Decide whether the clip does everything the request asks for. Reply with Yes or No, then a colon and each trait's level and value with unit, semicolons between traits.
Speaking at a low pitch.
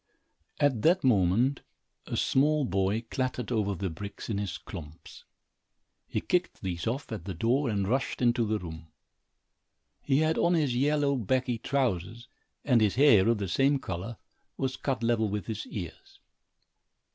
Yes: low, 115 Hz